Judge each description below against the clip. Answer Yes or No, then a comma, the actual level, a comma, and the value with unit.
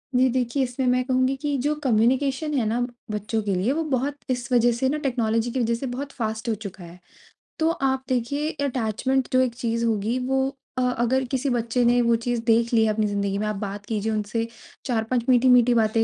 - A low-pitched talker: No, high, 240 Hz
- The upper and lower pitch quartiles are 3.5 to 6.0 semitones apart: No, average, 2.8 semitones